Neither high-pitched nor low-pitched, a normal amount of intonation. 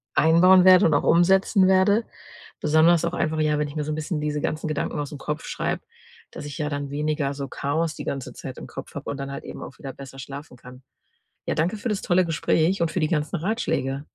Yes: medium, 155 Hz; average, 3.3 semitones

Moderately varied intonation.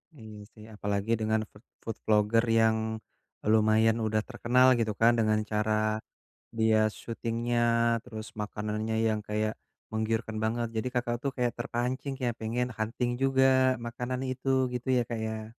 No: narrow, 1.8 semitones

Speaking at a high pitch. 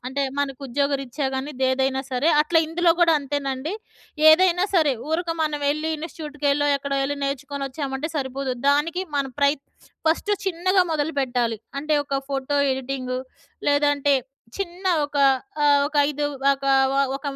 Yes: very high, 285 Hz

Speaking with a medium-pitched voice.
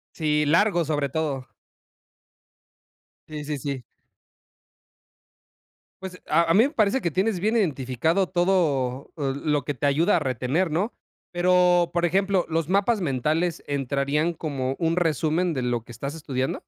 Yes: medium, 160 Hz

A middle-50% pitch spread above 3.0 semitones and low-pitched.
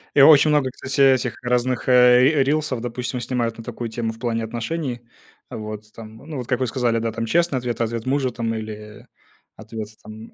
No: narrow, 2.6 semitones; low, 120 Hz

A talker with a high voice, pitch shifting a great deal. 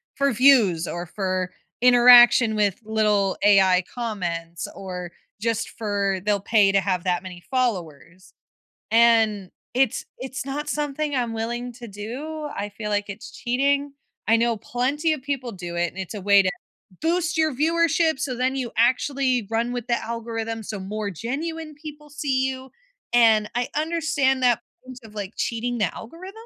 No: high, 235 Hz; average, 4.9 semitones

